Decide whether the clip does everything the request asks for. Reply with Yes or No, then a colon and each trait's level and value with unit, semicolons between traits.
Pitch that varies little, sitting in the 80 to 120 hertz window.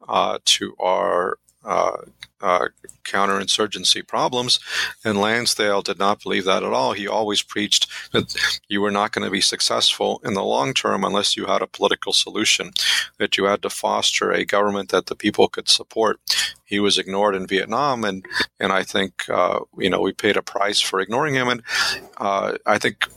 Yes: narrow, 1.2 semitones; low, 100 Hz